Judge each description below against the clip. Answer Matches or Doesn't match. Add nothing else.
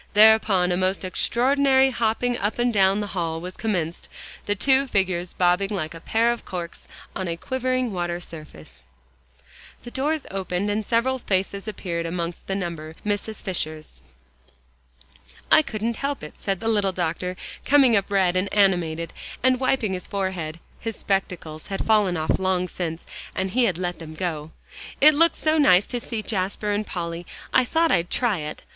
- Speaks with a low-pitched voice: Doesn't match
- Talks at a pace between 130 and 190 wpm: Matches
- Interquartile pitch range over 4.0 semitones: Matches